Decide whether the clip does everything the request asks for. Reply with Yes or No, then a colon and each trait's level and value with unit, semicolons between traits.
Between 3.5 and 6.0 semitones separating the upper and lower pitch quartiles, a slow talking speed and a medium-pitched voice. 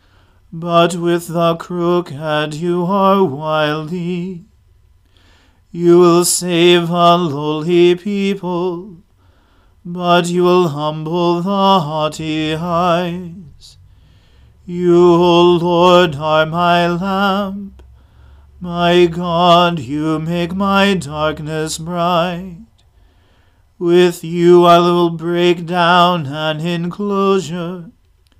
No: narrow, 2.4 semitones; slow, 90 wpm; medium, 175 Hz